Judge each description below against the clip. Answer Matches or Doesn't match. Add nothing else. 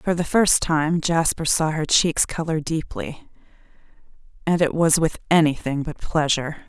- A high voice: Doesn't match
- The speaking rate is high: Doesn't match